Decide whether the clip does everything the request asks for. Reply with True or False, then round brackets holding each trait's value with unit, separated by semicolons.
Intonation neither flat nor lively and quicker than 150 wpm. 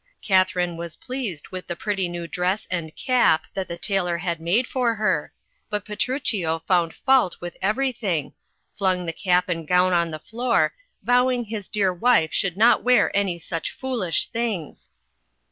True (4.9 semitones; 165 wpm)